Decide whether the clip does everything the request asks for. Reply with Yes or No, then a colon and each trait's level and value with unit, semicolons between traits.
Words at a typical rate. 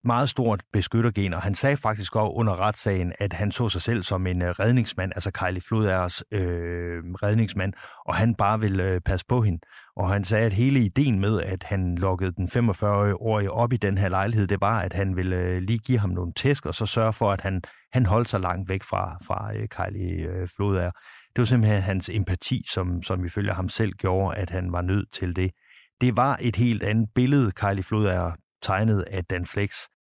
Yes: average, 200 wpm